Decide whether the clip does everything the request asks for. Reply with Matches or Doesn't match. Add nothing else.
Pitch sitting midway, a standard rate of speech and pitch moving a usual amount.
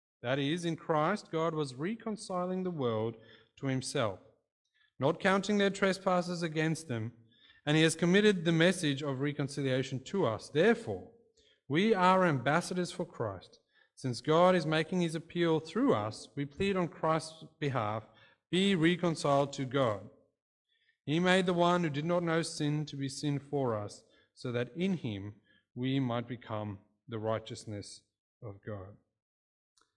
Doesn't match